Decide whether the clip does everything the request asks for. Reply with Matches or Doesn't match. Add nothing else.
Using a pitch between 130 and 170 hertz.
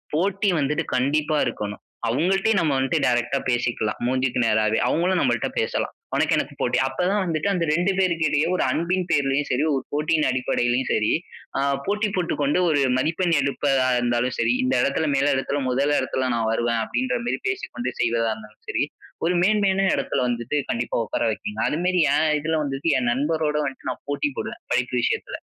Matches